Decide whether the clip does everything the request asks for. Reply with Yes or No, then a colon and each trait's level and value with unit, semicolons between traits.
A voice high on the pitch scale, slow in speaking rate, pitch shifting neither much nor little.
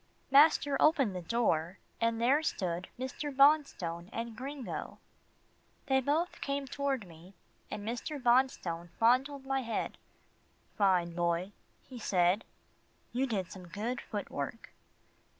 No: high, 235 Hz; slow, 125 wpm; wide, 6.9 semitones